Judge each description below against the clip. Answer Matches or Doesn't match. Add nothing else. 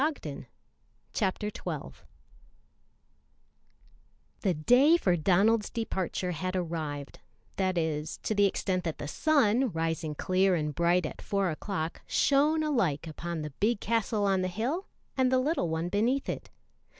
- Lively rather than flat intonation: Matches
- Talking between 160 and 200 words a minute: Doesn't match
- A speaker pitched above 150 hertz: Matches